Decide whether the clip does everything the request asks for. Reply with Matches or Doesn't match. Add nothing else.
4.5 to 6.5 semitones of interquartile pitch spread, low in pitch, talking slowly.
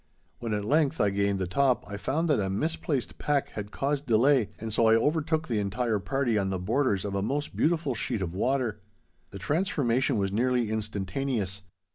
Doesn't match